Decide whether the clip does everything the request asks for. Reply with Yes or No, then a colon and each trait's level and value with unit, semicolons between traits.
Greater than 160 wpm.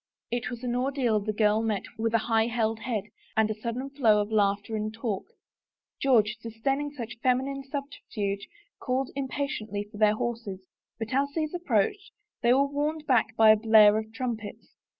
Yes: average, 175 wpm